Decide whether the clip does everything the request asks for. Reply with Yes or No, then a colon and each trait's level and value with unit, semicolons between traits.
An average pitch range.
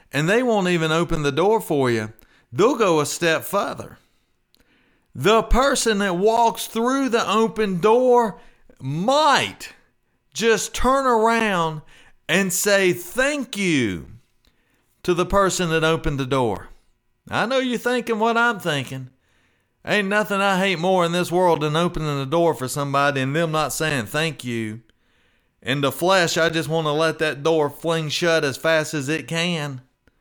No: wide, 6.7 semitones